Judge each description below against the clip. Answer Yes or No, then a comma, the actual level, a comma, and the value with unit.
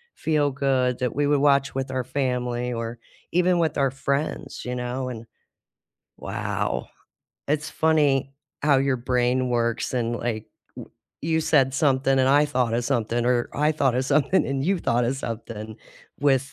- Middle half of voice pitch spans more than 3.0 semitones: No, average, 2.7 semitones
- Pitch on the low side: Yes, low, 130 Hz